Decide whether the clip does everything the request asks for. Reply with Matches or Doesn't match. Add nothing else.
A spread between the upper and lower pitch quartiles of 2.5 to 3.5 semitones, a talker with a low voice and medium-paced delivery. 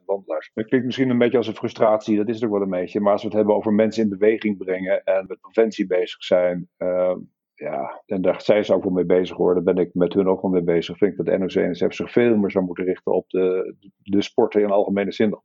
Doesn't match